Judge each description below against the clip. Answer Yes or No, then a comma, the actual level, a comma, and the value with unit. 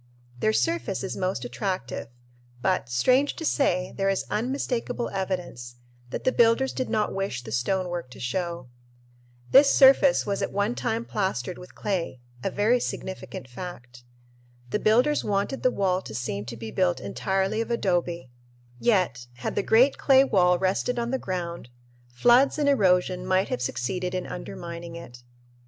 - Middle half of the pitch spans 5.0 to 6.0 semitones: Yes, wide, 5.5 semitones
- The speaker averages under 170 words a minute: Yes, average, 160 wpm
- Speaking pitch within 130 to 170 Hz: No, high, 190 Hz